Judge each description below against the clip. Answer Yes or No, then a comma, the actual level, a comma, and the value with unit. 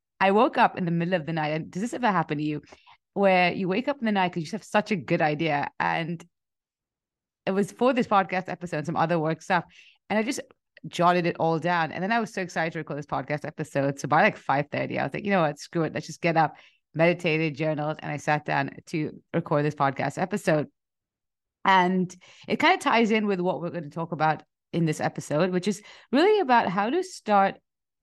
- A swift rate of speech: Yes, fast, 235 wpm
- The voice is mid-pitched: Yes, medium, 170 Hz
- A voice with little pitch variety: No, average, 3.9 semitones